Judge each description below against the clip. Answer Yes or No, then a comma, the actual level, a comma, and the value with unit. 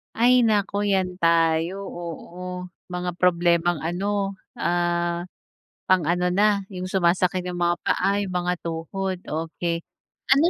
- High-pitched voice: No, medium, 180 Hz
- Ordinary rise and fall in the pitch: No, narrow, 2.1 semitones